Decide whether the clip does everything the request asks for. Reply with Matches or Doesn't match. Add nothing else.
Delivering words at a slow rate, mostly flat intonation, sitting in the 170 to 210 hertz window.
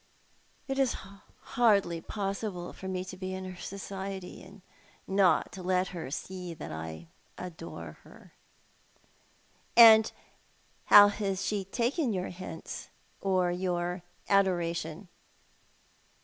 Matches